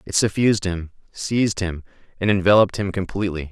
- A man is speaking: Yes, male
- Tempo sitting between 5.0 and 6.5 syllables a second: Yes, 6.3 syllables/s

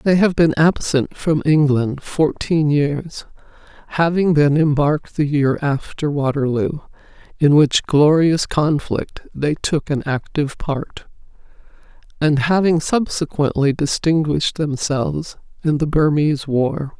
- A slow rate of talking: Yes, slow, 115 wpm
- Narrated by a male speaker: No, female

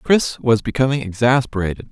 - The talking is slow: Yes, slow, 125 wpm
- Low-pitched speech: Yes, low, 125 Hz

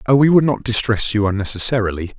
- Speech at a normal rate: Yes, average, 190 wpm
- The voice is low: Yes, low, 115 Hz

